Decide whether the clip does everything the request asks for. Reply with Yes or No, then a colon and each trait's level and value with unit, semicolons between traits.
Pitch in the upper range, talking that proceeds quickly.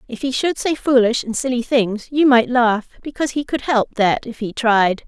Yes: high, 245 Hz; fast, 225 wpm